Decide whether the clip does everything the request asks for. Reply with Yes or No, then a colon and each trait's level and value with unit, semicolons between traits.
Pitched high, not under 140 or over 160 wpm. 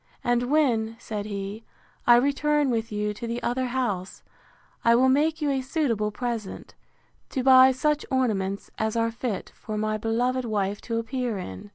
No: high, 235 Hz; average, 175 wpm